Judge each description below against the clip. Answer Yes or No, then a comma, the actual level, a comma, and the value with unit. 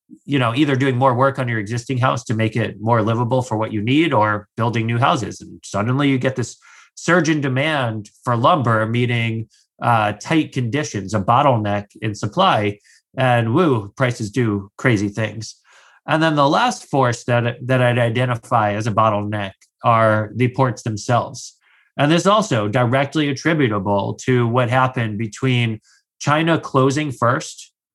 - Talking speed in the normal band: Yes, average, 165 wpm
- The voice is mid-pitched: No, low, 120 Hz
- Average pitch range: Yes, average, 3.6 semitones